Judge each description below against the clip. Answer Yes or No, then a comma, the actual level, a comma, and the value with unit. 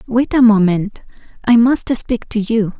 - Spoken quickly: No, average, 170 wpm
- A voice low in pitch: No, high, 225 Hz